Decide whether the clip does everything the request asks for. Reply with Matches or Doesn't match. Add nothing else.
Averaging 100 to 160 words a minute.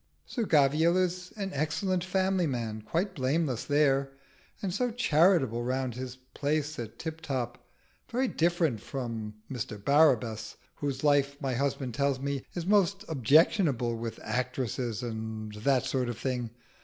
Matches